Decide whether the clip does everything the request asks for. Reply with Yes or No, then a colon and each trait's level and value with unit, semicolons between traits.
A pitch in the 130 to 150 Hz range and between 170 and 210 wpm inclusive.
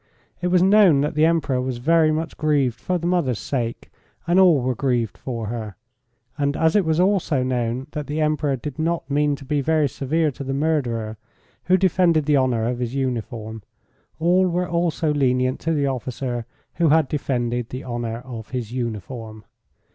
Yes: medium, 140 Hz; average, 185 wpm